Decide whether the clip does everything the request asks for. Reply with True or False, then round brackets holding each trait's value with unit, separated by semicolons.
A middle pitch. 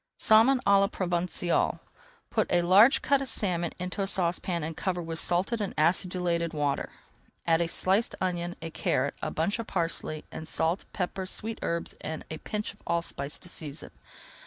True (175 Hz)